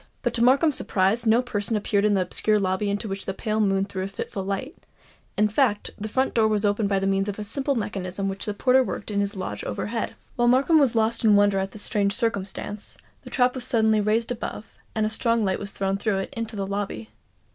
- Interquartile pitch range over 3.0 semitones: No, average, 2.7 semitones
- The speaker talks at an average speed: No, fast, 235 wpm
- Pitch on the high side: Yes, high, 210 Hz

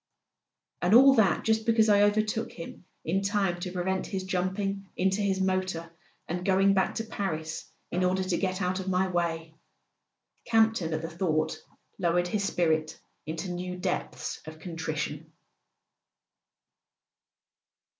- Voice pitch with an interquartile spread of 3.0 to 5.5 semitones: No, narrow, 2.6 semitones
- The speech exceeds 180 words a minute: No, average, 145 wpm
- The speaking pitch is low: No, medium, 185 Hz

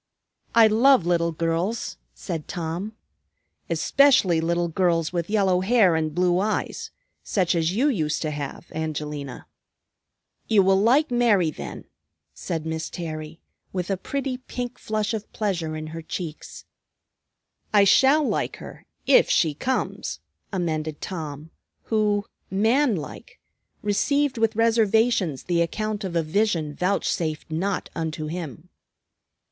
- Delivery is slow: Yes, slow, 130 wpm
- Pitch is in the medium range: Yes, medium, 180 Hz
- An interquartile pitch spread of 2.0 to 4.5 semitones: No, average, 5.2 semitones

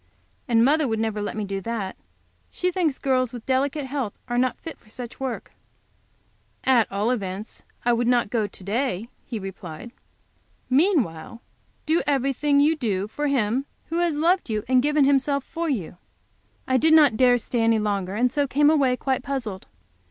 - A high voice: Yes, very high, 250 Hz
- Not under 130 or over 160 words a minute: No, average, 180 wpm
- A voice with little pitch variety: No, average, 4.7 semitones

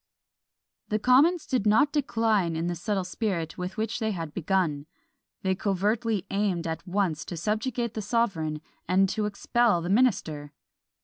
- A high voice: Yes, high, 200 Hz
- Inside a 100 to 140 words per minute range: No, average, 150 wpm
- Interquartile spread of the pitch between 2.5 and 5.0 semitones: Yes, average, 4.5 semitones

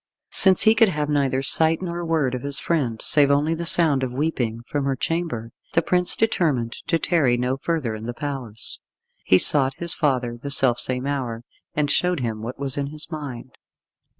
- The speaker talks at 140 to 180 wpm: No, average, 195 wpm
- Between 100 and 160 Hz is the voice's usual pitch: Yes, medium, 140 Hz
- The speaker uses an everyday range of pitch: Yes, average, 4.5 semitones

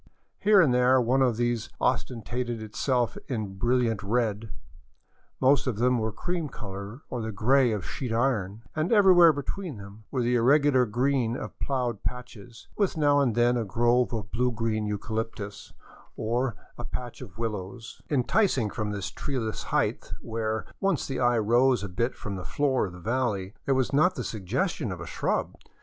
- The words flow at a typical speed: Yes, average, 175 wpm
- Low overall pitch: Yes, low, 120 Hz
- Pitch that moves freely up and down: No, average, 3.3 semitones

